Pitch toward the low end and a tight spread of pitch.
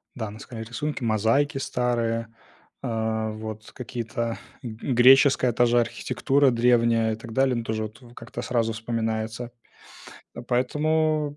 Yes: low, 120 Hz; narrow, 2.2 semitones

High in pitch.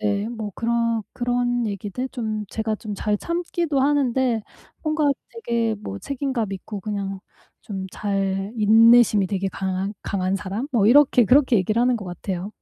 Yes: high, 220 Hz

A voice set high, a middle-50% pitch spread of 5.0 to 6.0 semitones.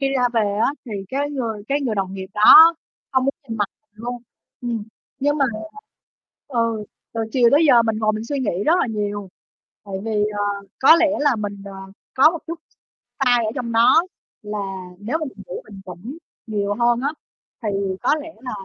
No: high, 230 Hz; average, 4.6 semitones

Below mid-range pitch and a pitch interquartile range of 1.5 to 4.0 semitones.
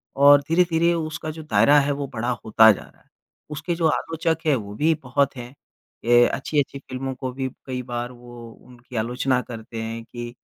Yes: low, 130 Hz; average, 3.7 semitones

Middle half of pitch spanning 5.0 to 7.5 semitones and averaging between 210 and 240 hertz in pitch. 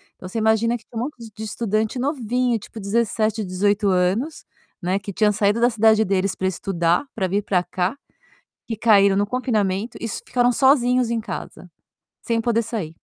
No: average, 3.1 semitones; high, 220 Hz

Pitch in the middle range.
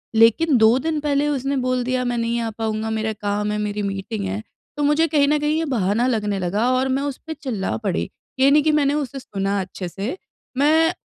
No: high, 245 Hz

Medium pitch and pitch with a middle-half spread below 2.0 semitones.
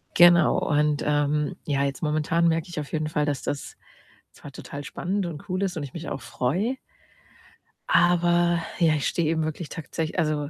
No: medium, 155 Hz; average, 2.8 semitones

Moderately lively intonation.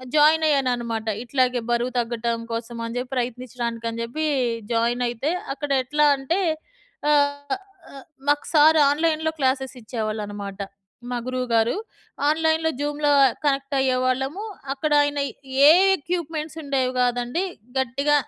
Yes: average, 3.7 semitones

